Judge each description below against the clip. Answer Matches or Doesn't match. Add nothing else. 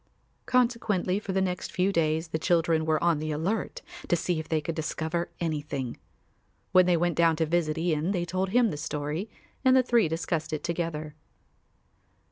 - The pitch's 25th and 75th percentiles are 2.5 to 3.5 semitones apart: Matches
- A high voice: Doesn't match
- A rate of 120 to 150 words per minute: Doesn't match